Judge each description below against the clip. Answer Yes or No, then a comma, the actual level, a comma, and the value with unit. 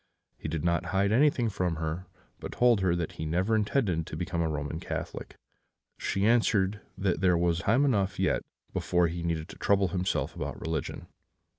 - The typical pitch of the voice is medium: No, very low, 90 Hz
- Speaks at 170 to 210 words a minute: Yes, average, 175 wpm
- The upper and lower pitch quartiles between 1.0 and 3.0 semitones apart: No, average, 3.4 semitones